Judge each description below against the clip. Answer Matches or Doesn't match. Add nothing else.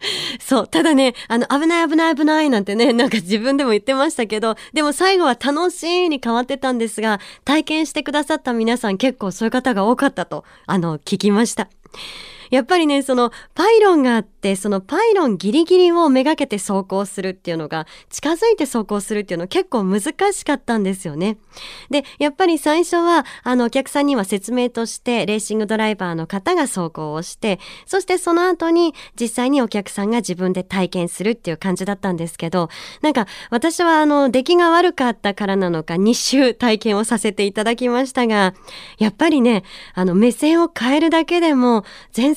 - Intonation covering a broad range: Matches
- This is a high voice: Matches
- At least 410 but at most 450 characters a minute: Doesn't match